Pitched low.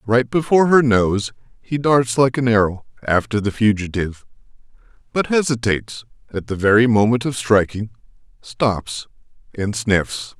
Yes: low, 115 Hz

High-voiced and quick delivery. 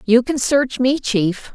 No: high, 245 Hz; average, 195 wpm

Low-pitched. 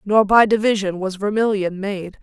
No: high, 200 Hz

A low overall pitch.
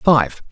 Yes: low, 120 Hz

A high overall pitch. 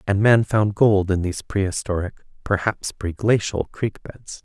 No: low, 100 Hz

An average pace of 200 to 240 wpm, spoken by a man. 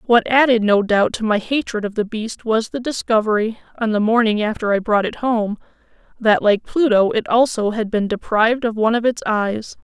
No: fast, 205 wpm; female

